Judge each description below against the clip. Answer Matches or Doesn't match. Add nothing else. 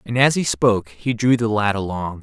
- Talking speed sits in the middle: Doesn't match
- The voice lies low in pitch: Matches